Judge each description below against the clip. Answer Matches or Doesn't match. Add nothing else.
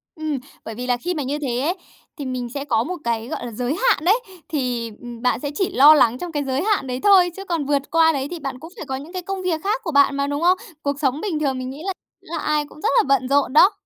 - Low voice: Doesn't match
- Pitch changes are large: Doesn't match